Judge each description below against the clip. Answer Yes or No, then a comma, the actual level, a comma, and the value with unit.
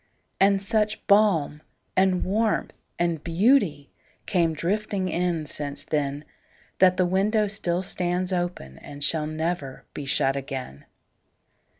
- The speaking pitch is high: No, medium, 175 Hz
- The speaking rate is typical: No, slow, 105 wpm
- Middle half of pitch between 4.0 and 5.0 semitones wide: Yes, average, 4.6 semitones